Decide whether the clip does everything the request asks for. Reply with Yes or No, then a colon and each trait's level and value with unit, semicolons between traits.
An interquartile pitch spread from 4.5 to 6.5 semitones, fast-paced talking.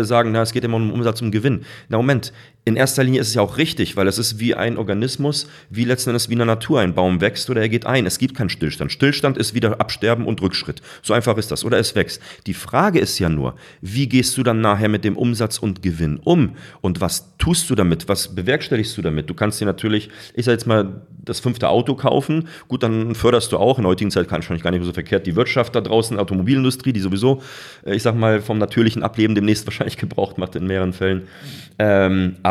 No: average, 4.0 semitones; fast, 245 wpm